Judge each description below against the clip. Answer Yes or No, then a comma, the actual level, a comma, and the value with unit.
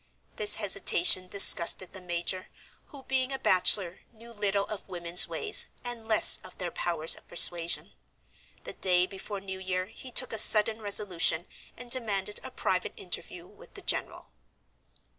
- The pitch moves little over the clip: No, average, 3.7 semitones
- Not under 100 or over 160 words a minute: Yes, average, 155 wpm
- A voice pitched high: Yes, high, 195 Hz